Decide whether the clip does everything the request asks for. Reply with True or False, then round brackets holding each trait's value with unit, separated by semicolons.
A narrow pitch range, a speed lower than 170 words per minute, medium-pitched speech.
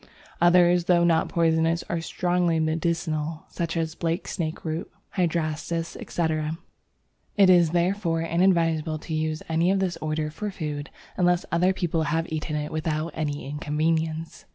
True (1.7 semitones; 140 wpm; 165 Hz)